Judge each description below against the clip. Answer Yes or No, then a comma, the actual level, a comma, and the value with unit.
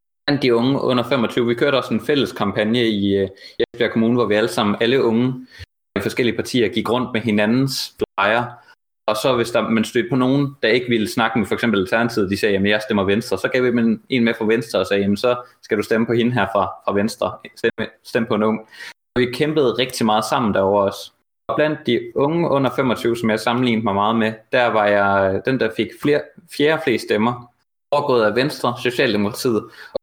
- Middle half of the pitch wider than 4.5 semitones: No, average, 2.9 semitones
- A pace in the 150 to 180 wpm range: No, average, 220 wpm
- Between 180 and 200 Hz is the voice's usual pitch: No, low, 115 Hz